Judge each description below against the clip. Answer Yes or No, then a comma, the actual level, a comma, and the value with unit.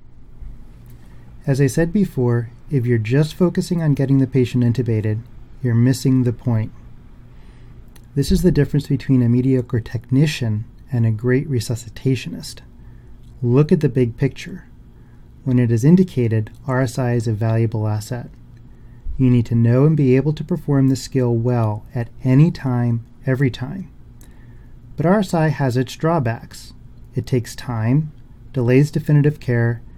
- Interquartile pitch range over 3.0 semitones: No, average, 2.7 semitones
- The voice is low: Yes, low, 125 Hz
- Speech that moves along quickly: No, average, 140 wpm